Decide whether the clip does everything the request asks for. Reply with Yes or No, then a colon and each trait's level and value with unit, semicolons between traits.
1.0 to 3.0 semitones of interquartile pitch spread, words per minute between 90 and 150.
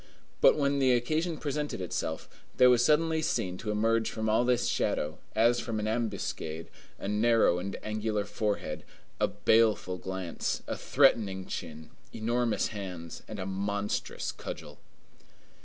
No: average, 4.2 semitones; average, 140 wpm